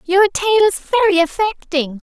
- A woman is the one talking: Yes, female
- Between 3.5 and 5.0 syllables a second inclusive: Yes, 4.2 syllables/s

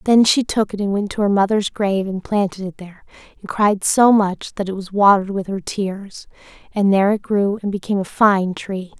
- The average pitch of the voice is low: No, high, 200 Hz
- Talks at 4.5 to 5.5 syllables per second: Yes, 5.4 syllables/s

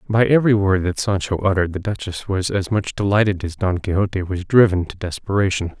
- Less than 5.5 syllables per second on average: No, 5.9 syllables/s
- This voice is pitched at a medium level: No, very low, 95 Hz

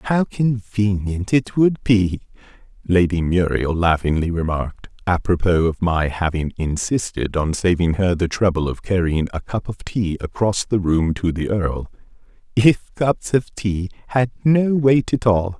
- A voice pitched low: Yes, very low, 95 Hz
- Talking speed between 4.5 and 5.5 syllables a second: No, 4.2 syllables/s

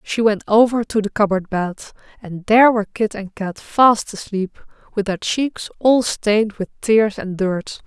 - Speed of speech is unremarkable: Yes, average, 185 wpm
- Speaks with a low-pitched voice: No, high, 210 Hz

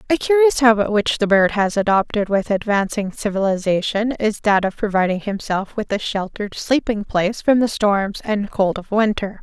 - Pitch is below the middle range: No, high, 210 Hz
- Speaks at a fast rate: No, average, 180 wpm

